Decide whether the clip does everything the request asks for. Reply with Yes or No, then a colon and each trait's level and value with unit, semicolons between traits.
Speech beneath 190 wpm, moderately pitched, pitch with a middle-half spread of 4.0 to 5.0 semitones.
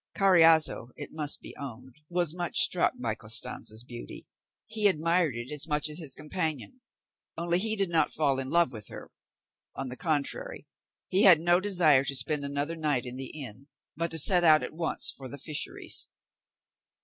Yes: average, 180 wpm; medium, 155 Hz; average, 4.3 semitones